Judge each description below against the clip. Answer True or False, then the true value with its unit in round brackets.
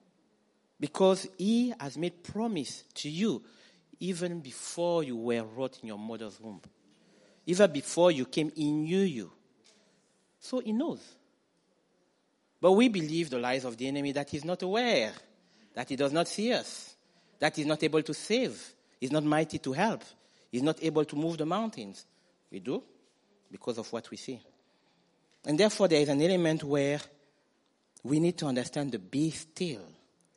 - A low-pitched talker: False (160 Hz)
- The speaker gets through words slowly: False (165 wpm)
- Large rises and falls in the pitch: False (4.9 semitones)